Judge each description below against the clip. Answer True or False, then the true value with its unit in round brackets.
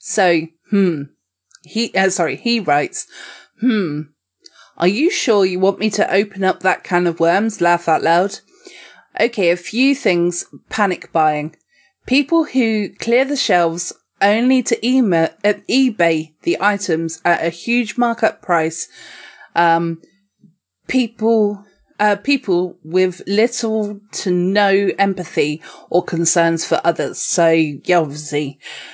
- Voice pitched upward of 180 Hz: True (190 Hz)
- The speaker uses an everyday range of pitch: True (4.7 semitones)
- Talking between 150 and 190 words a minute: False (135 wpm)